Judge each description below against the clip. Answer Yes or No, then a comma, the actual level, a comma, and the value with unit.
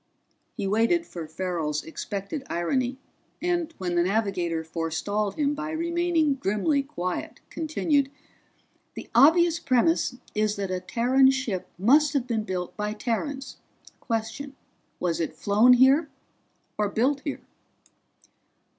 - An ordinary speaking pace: No, slow, 125 wpm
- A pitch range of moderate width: No, wide, 7.0 semitones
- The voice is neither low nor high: No, high, 235 Hz